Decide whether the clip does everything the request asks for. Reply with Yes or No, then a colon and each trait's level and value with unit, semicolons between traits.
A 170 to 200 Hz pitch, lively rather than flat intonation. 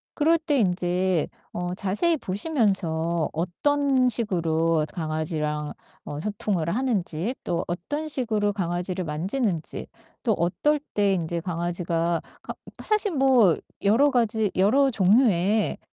Yes: high, 190 Hz; wide, 6.4 semitones